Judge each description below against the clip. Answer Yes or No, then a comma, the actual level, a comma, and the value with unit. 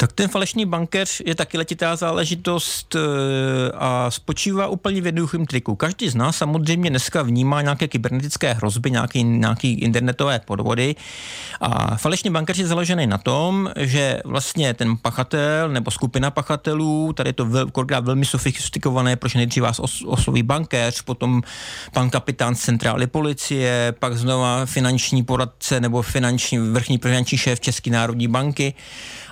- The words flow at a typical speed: Yes, average, 145 wpm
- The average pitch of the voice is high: No, low, 130 Hz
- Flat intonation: No, average, 4.0 semitones